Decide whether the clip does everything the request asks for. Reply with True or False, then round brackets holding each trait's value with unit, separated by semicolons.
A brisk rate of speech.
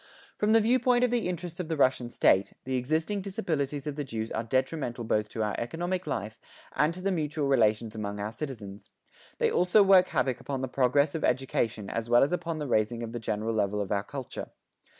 True (210 wpm)